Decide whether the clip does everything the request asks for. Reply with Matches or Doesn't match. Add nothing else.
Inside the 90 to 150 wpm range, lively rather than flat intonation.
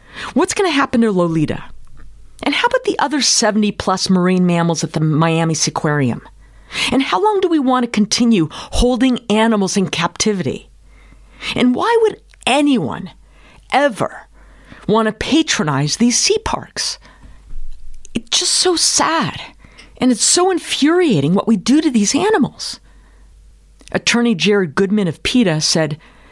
Matches